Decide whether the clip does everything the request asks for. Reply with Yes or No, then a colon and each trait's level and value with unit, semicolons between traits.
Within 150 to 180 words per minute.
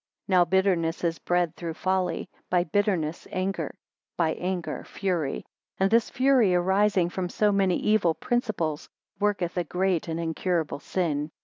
No: average, 140 wpm